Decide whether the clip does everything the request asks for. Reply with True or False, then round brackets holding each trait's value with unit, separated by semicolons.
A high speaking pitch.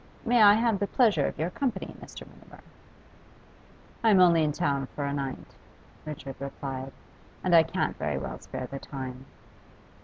False (155 Hz)